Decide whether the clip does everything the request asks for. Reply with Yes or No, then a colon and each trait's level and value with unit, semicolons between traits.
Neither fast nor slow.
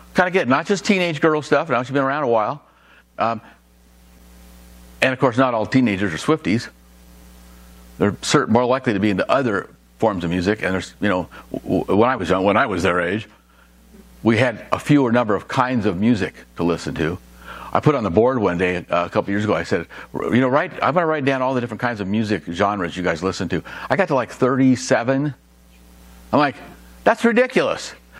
No: fast, 215 wpm